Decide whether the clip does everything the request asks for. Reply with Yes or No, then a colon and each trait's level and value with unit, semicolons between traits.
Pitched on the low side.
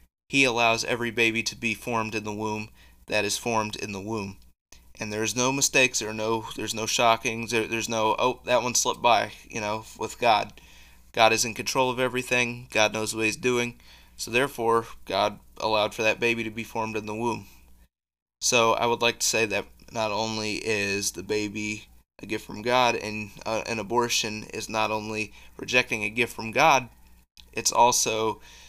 Yes: low, 110 Hz